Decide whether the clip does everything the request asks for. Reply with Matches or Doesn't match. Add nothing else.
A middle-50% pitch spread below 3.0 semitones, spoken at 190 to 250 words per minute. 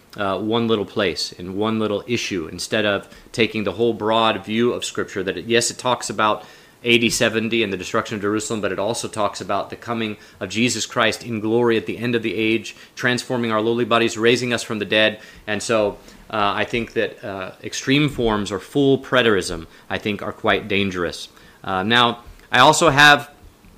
Matches